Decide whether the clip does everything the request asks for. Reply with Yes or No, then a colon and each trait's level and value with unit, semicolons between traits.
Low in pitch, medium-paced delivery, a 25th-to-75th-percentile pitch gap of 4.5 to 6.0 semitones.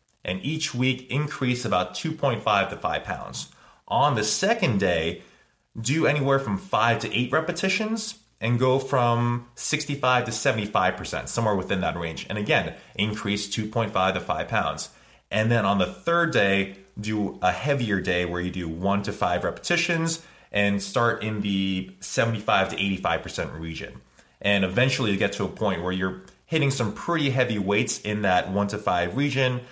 Yes: low, 110 Hz; average, 165 wpm; wide, 5.5 semitones